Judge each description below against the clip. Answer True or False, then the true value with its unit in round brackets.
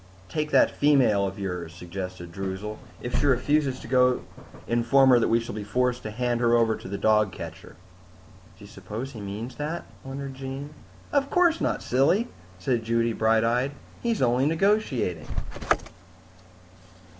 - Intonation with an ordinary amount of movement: True (4.5 semitones)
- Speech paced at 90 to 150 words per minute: False (160 wpm)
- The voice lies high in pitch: False (120 Hz)